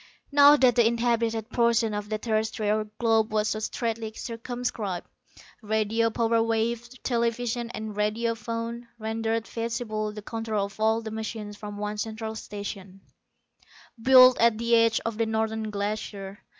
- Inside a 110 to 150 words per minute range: Yes, average, 145 wpm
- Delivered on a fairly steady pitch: Yes, narrow, 1.5 semitones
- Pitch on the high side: Yes, high, 225 Hz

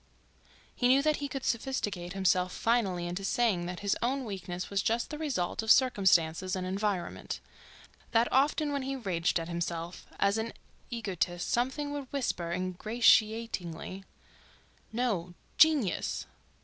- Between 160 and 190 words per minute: No, slow, 135 wpm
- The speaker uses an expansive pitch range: Yes, wide, 5.7 semitones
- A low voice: No, high, 205 Hz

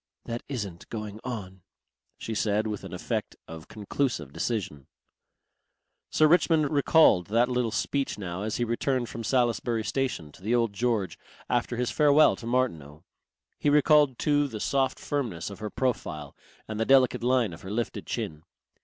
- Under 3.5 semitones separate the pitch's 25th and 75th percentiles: No, average, 4.6 semitones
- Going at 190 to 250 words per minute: No, average, 160 wpm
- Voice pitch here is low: Yes, low, 115 Hz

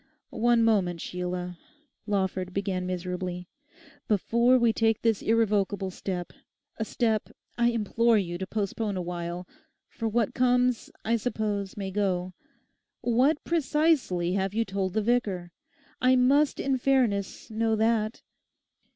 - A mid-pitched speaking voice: No, high, 210 Hz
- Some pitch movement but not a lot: Yes, average, 4.2 semitones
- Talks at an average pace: No, slow, 120 wpm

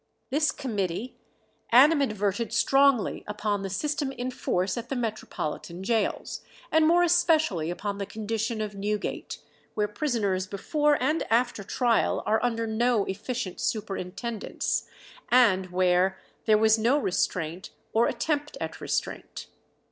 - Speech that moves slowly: Yes, slow, 125 wpm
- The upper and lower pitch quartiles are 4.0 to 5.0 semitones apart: Yes, average, 4.4 semitones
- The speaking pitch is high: Yes, high, 220 Hz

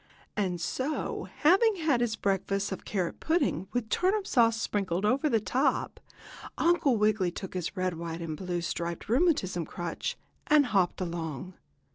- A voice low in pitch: No, high, 205 Hz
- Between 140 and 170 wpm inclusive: Yes, average, 150 wpm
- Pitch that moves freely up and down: Yes, wide, 7.3 semitones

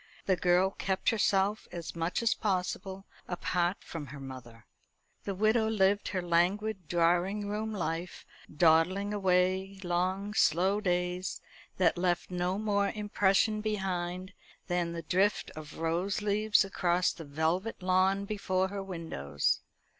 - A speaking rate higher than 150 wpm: No, slow, 135 wpm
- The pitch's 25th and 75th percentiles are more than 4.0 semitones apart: No, narrow, 2.5 semitones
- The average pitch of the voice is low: No, medium, 185 Hz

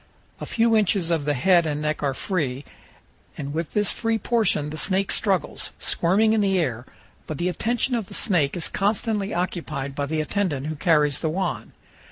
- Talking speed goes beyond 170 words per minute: Yes, average, 190 wpm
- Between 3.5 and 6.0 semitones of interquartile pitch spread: Yes, average, 5.2 semitones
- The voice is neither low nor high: Yes, medium, 170 Hz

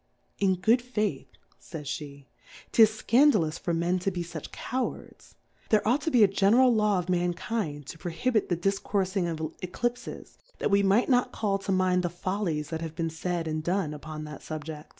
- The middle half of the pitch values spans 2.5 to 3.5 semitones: No, average, 4.6 semitones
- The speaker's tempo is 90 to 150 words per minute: No, average, 175 wpm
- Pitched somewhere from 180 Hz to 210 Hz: Yes, medium, 185 Hz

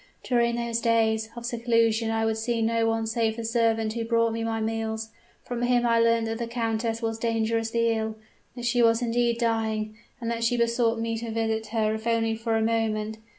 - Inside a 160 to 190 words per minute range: No, fast, 205 wpm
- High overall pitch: Yes, high, 230 Hz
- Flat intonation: Yes, narrow, 0.8 semitones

